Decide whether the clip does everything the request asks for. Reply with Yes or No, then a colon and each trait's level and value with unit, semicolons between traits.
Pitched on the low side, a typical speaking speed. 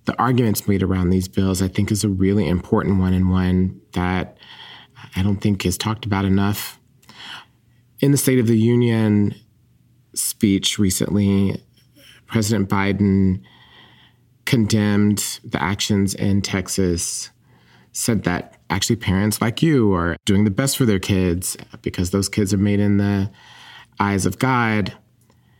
Yes: low, 100 Hz; average, 145 wpm